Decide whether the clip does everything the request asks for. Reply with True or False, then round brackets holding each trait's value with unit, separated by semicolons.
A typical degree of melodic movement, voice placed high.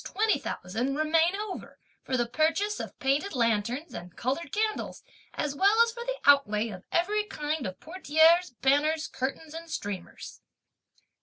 False (6.4 semitones; 310 Hz)